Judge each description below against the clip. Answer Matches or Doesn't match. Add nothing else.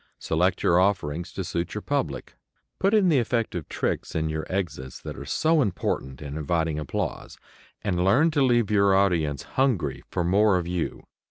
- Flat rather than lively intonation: Doesn't match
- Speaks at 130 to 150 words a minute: Doesn't match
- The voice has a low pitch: Matches